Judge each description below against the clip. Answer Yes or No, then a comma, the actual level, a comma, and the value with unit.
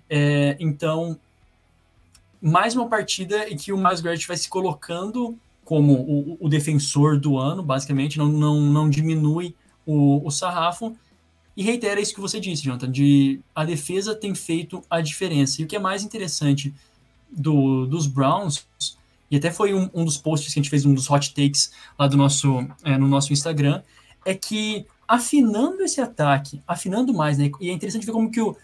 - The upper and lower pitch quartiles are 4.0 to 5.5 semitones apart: Yes, average, 5.0 semitones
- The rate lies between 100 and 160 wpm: No, average, 180 wpm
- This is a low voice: No, medium, 155 Hz